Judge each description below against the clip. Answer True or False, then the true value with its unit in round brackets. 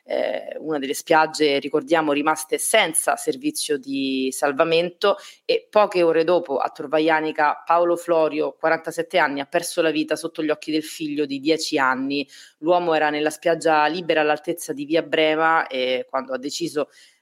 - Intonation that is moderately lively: False (2.1 semitones)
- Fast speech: False (155 wpm)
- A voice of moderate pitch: True (155 Hz)